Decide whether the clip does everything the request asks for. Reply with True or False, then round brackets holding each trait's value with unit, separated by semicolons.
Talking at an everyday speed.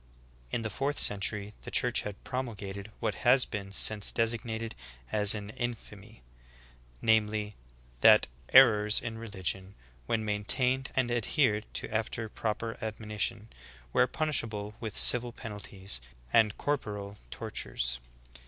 False (130 wpm)